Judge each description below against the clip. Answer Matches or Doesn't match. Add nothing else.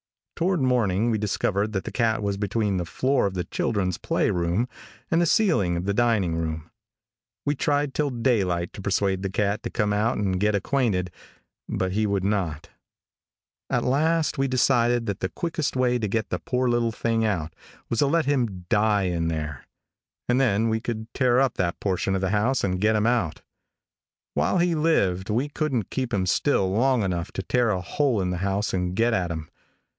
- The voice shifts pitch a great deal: Doesn't match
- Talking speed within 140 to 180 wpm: Doesn't match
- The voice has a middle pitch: Doesn't match